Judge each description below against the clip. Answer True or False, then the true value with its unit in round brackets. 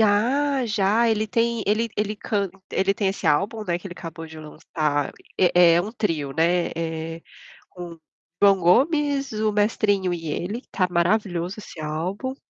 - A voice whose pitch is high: True (195 Hz)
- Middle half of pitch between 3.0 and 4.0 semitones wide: False (4.4 semitones)